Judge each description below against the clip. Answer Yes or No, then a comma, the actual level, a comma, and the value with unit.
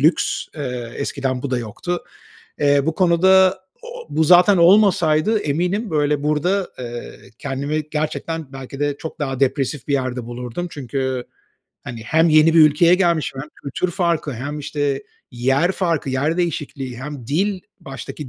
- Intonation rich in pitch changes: No, average, 4.2 semitones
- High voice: No, medium, 150 Hz